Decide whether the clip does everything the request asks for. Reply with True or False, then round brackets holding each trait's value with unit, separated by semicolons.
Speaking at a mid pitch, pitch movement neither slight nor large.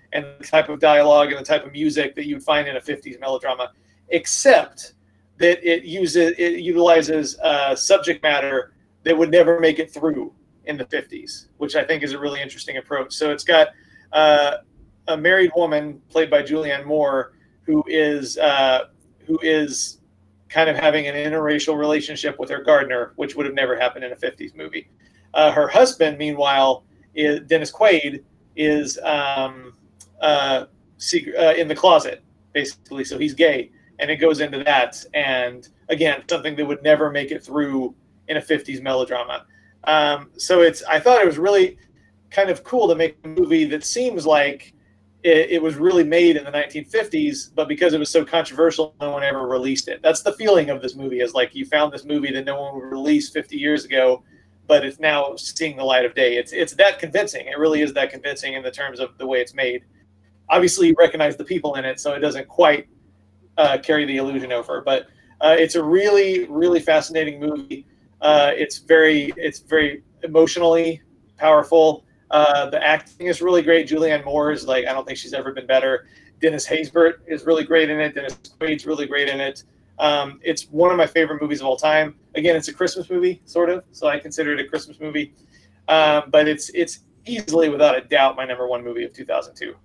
True (150 Hz; 3.1 semitones)